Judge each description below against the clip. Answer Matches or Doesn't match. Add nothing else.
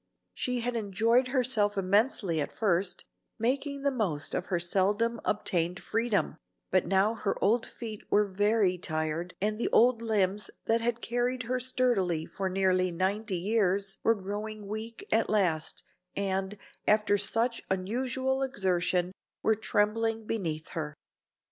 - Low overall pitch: Doesn't match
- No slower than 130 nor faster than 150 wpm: Matches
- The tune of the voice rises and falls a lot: Doesn't match